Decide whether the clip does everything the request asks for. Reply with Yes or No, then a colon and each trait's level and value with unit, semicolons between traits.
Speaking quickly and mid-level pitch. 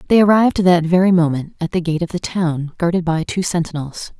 Yes: fast, 215 wpm; medium, 170 Hz